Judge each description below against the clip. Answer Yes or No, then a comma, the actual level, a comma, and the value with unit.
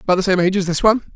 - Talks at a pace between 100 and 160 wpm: No, fast, 365 wpm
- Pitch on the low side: No, high, 190 Hz